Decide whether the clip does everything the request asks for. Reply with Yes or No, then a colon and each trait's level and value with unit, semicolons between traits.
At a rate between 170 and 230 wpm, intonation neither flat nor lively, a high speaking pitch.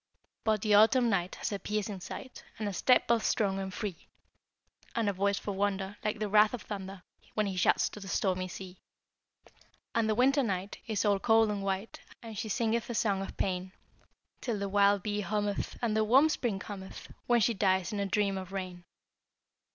No: fast, 205 wpm; narrow, 2.2 semitones; high, 205 Hz